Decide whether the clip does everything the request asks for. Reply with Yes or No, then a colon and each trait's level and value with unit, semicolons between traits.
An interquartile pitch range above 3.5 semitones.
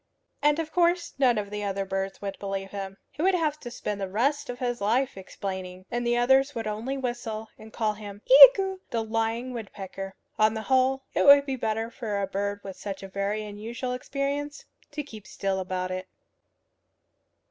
Yes: average, 5.1 semitones